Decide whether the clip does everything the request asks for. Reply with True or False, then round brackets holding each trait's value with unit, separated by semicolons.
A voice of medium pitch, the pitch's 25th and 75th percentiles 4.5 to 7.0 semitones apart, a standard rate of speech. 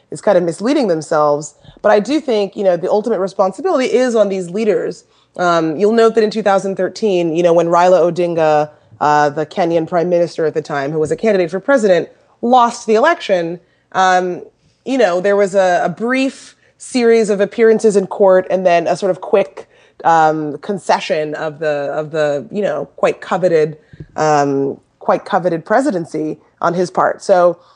True (180 Hz; 4.9 semitones; 185 wpm)